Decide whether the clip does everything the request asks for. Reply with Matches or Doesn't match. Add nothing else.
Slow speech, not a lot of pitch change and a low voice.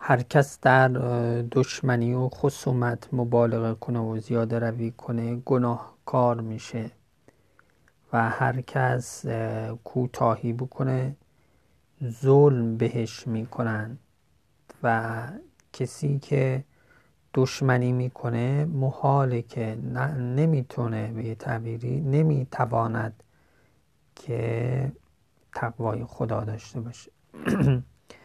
Matches